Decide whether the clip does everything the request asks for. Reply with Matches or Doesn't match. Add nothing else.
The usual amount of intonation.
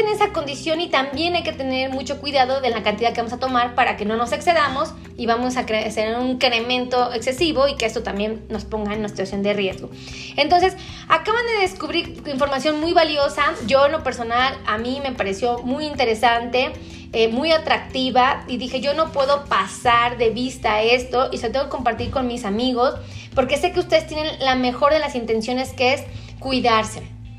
Matches